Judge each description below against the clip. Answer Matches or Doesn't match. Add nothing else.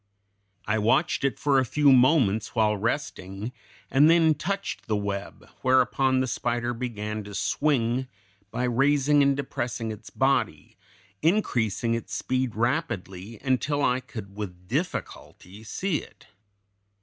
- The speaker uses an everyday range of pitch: Matches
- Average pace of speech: Doesn't match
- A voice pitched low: Matches